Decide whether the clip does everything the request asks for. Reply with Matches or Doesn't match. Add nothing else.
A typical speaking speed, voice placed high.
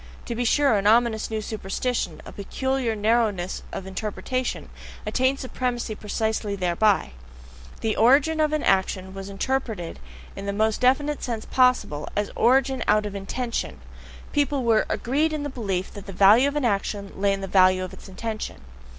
Matches